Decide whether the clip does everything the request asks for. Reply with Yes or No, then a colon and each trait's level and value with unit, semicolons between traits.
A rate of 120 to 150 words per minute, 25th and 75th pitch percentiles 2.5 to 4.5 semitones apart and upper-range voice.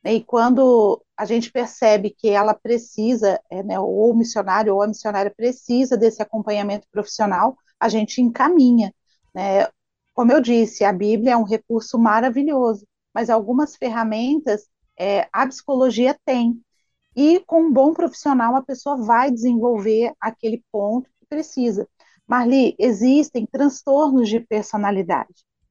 Yes: average, 135 wpm; average, 3.3 semitones; high, 235 Hz